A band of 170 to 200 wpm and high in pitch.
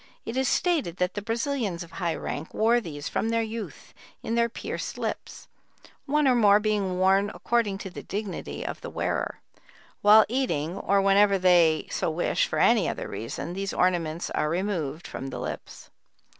Yes: average, 175 wpm; high, 195 Hz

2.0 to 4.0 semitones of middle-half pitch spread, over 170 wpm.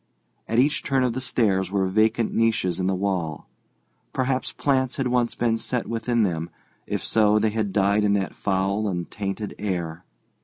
Yes: average, 3.7 semitones; average, 180 wpm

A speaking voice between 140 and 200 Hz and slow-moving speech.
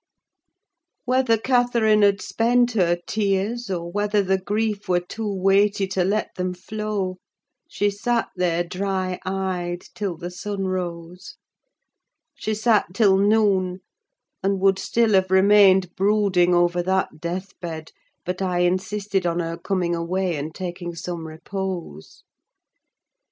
Yes: high, 190 Hz; slow, 130 wpm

